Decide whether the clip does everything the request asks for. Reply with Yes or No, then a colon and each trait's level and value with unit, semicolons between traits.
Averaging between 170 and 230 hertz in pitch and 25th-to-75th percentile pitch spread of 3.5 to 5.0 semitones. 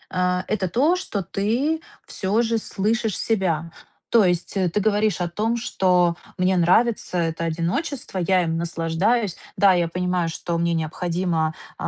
Yes: medium, 185 Hz; average, 4.1 semitones